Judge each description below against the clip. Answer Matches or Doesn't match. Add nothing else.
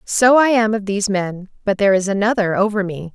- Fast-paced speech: Matches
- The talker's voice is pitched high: Matches